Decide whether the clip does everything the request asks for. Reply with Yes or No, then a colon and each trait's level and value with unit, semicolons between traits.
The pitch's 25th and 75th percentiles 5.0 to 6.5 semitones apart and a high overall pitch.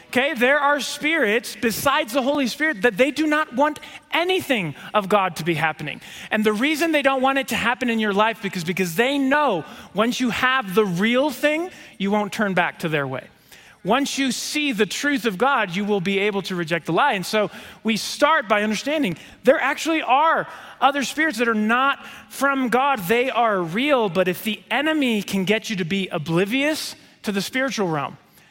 Yes: average, 5.3 semitones; high, 235 Hz